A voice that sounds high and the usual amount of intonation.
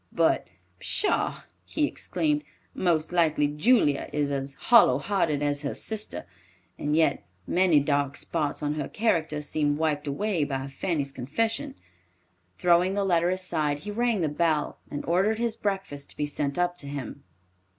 No: medium, 155 Hz; average, 4.8 semitones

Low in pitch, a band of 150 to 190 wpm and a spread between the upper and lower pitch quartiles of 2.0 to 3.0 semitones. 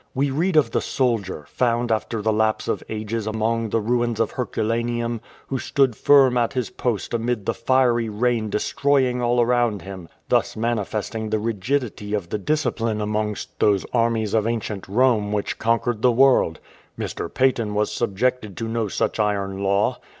Yes: low, 115 Hz; average, 165 wpm; narrow, 2.6 semitones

